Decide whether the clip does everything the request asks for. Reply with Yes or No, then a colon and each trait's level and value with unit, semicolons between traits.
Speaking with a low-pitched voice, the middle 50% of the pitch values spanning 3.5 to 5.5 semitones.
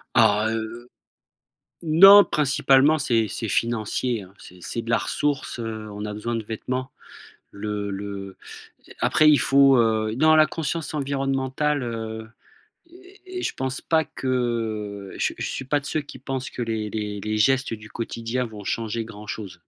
Yes: low, 115 Hz; average, 4.1 semitones